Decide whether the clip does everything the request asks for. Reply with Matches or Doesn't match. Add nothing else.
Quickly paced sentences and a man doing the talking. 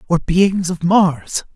Doesn't match